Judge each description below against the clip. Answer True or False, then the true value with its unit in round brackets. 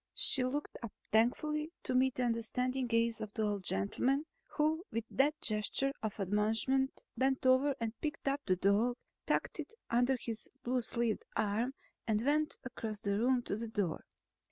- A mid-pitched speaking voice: False (240 Hz)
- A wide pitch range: False (3.6 semitones)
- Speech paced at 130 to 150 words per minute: False (170 wpm)